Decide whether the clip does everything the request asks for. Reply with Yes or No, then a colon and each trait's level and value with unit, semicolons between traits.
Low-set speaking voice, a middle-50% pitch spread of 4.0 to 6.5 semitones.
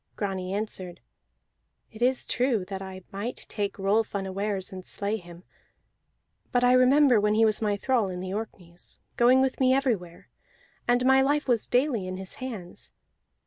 No: high, 210 Hz; average, 4.8 semitones